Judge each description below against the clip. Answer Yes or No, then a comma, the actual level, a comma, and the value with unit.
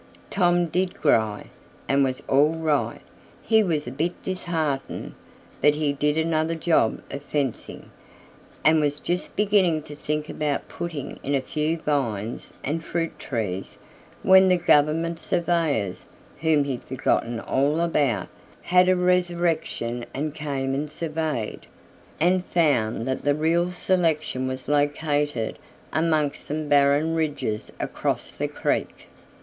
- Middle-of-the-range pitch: Yes, medium, 150 Hz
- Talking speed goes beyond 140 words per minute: No, slow, 135 wpm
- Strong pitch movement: No, average, 3.1 semitones